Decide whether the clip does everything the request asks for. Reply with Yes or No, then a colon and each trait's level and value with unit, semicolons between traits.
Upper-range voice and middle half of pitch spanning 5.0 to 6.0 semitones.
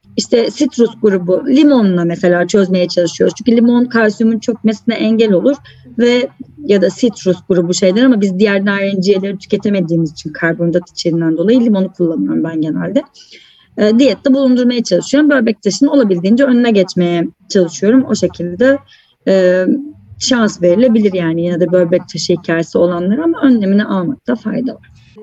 Yes: high, 205 Hz; average, 5.3 semitones